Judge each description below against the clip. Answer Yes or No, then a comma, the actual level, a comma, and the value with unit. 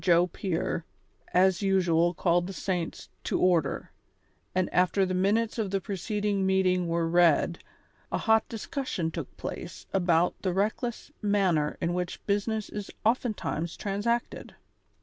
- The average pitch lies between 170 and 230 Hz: Yes, medium, 185 Hz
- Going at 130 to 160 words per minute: Yes, slow, 135 wpm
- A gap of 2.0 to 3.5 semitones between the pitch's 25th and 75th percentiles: Yes, average, 2.9 semitones